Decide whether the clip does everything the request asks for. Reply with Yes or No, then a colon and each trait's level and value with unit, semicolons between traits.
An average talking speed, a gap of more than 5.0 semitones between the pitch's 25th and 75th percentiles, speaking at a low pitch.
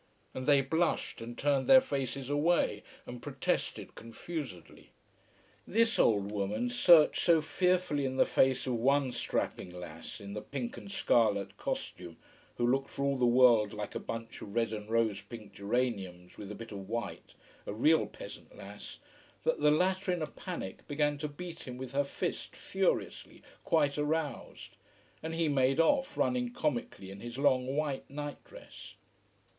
Yes: average, 165 wpm; wide, 5.5 semitones; low, 130 Hz